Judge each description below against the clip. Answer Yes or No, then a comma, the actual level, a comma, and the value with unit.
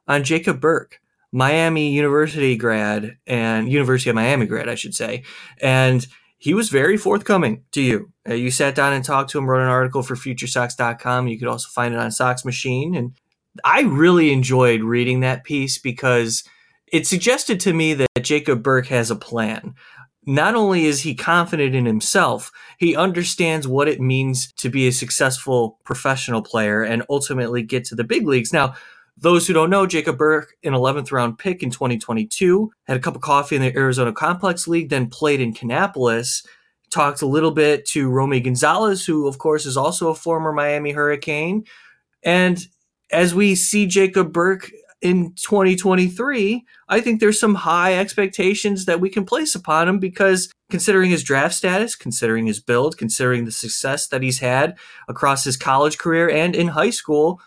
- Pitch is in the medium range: Yes, medium, 145 Hz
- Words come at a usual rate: Yes, average, 175 wpm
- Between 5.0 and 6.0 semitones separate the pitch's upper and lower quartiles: Yes, wide, 5.4 semitones